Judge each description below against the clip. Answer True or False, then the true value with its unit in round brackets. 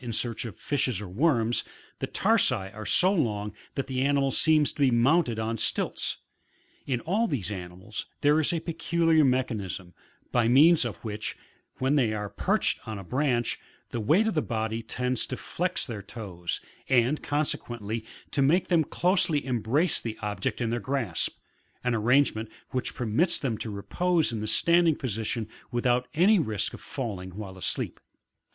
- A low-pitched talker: True (120 Hz)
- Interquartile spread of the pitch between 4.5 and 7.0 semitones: True (5.4 semitones)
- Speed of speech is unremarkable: True (170 wpm)